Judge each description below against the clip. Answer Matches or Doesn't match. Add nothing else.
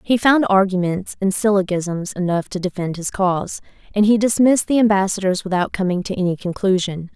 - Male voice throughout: Doesn't match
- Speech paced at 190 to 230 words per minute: Doesn't match